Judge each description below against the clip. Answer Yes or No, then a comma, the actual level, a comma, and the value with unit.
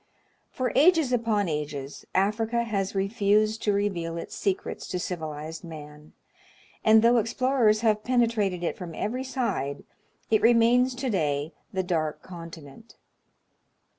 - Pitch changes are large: Yes, wide, 5.8 semitones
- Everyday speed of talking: No, slow, 130 wpm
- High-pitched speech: Yes, high, 205 Hz